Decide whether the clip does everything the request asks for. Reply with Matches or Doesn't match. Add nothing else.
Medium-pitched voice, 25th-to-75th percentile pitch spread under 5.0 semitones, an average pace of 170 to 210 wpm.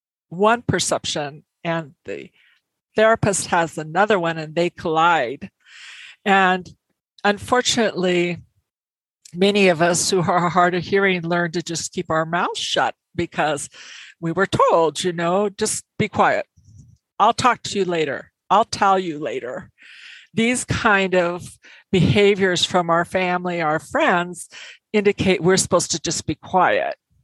Doesn't match